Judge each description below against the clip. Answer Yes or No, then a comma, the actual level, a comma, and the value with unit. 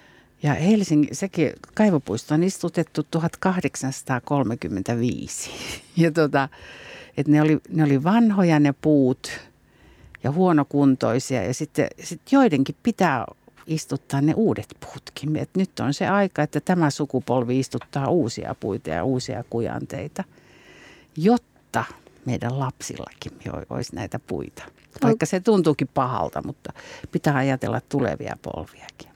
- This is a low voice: No, medium, 145 Hz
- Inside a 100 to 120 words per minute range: Yes, average, 115 wpm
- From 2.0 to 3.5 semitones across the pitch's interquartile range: No, average, 4.5 semitones